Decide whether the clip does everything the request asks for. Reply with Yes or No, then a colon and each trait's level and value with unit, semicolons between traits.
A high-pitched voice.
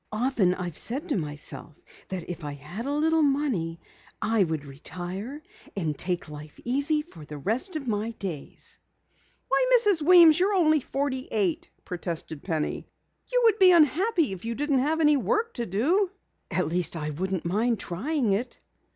Yes: high, 225 Hz